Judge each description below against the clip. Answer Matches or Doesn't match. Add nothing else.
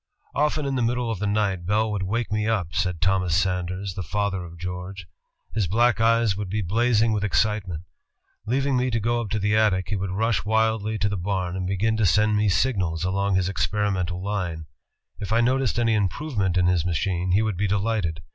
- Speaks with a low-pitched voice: Matches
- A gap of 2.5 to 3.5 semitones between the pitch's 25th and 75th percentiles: Matches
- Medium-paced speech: Doesn't match